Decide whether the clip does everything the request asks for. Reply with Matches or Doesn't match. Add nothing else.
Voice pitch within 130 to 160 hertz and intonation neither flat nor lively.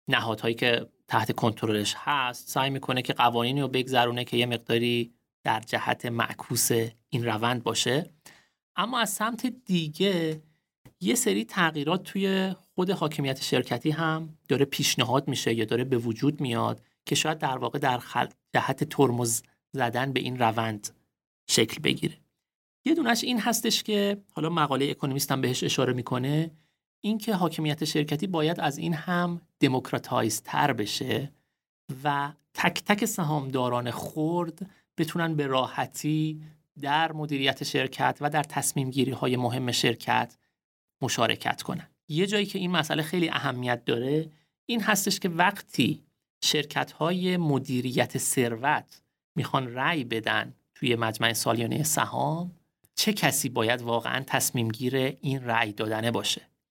Matches